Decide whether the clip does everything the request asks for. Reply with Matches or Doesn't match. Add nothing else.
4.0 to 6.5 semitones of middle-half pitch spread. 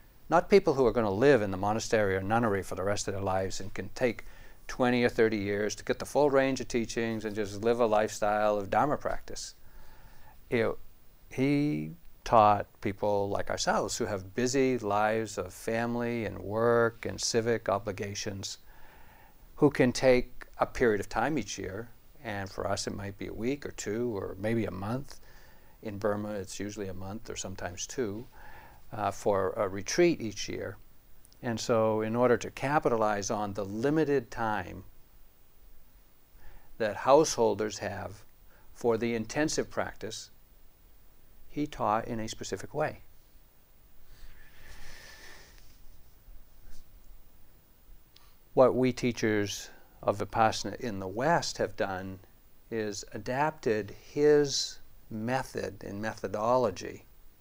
Doesn't match